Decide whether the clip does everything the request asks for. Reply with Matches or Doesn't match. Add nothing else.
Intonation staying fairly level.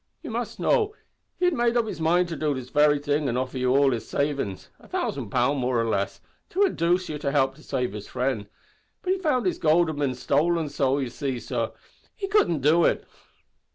Doesn't match